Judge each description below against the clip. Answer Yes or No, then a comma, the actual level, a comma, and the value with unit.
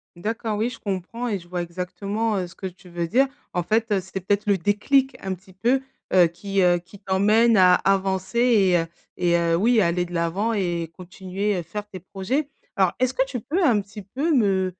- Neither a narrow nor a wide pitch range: Yes, average, 3.7 semitones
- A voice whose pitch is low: No, high, 195 Hz